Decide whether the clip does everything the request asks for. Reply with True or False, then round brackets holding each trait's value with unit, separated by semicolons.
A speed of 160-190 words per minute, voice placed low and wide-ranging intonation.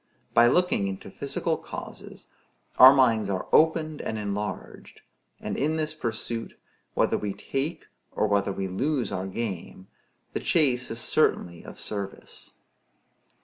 False (135 wpm; 115 Hz; 6.1 semitones)